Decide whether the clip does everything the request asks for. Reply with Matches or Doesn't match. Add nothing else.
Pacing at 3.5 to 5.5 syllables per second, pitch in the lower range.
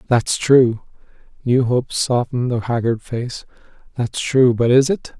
Matches